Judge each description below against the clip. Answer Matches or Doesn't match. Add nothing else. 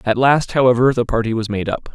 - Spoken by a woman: Doesn't match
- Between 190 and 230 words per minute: Doesn't match